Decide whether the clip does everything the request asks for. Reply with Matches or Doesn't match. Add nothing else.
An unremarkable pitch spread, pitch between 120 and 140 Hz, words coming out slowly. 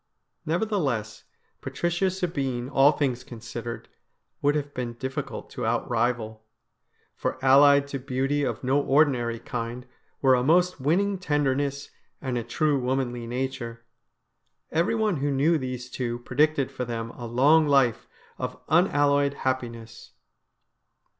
Matches